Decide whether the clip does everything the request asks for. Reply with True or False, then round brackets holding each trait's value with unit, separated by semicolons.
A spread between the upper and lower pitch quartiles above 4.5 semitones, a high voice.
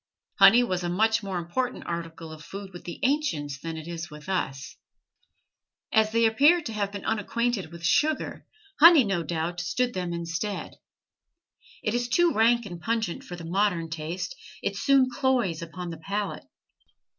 True (5.6 semitones; 195 Hz)